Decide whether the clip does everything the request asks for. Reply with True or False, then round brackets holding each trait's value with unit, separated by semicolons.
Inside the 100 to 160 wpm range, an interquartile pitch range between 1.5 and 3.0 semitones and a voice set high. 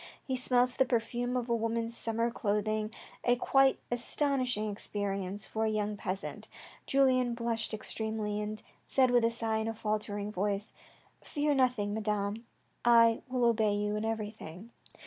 True (155 wpm; 2.5 semitones; 225 Hz)